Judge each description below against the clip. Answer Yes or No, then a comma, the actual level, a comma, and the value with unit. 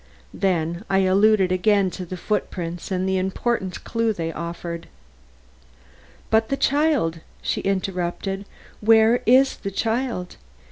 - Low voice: No, high, 195 Hz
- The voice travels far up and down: No, average, 3.7 semitones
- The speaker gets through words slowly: Yes, slow, 125 wpm